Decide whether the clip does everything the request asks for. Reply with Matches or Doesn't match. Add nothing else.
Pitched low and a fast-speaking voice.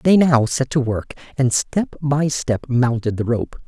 Doesn't match